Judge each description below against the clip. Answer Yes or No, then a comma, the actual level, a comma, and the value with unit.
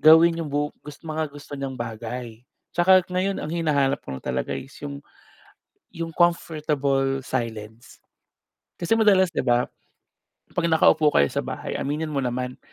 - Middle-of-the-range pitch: Yes, medium, 145 Hz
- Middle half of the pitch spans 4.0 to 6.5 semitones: Yes, average, 4.4 semitones